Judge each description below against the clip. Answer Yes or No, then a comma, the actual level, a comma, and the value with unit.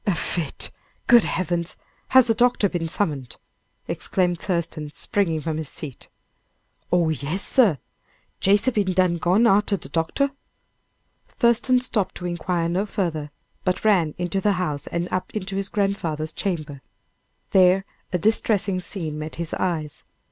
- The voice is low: No, medium, 180 Hz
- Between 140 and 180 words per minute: Yes, average, 145 wpm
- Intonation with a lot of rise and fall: No, average, 3.8 semitones